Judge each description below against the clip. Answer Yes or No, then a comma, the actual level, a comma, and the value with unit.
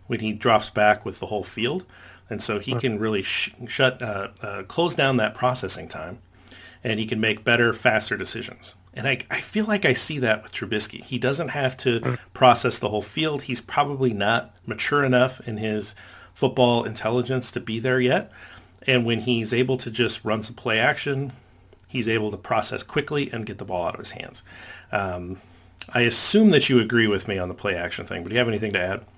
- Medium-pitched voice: No, low, 115 Hz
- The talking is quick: Yes, fast, 210 wpm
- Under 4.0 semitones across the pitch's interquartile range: Yes, average, 3.4 semitones